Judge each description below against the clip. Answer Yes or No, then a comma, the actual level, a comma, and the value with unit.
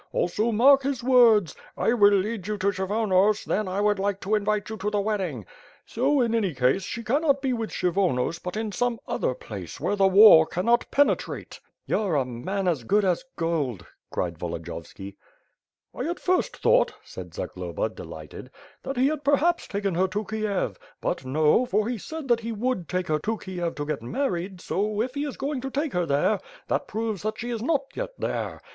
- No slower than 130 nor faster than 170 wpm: No, average, 200 wpm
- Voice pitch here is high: Yes, high, 210 Hz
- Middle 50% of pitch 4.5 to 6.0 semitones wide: Yes, average, 5.2 semitones